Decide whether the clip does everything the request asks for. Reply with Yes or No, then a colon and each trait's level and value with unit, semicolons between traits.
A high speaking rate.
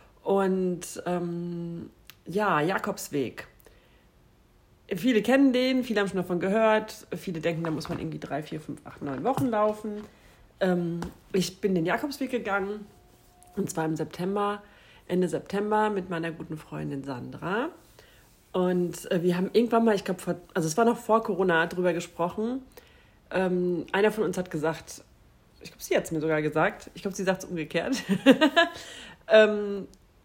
No: average, 155 wpm